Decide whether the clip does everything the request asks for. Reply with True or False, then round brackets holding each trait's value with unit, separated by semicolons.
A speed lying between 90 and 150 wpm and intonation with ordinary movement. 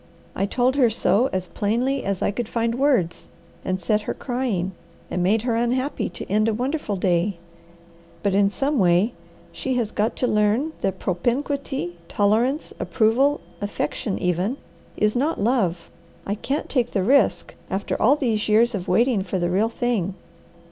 False (165 wpm; 4.5 semitones)